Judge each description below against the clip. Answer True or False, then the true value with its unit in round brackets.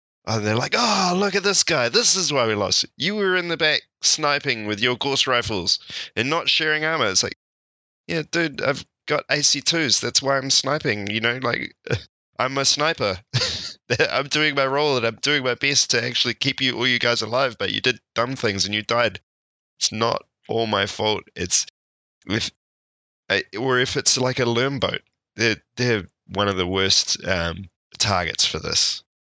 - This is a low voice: True (125 Hz)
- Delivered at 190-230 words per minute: True (195 wpm)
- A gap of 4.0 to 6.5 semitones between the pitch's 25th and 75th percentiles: True (5.6 semitones)